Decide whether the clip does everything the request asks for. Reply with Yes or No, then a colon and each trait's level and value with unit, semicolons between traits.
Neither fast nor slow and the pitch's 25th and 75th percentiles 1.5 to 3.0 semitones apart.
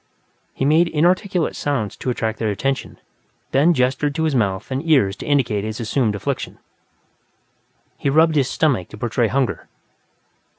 No: average, 155 wpm; wide, 5.4 semitones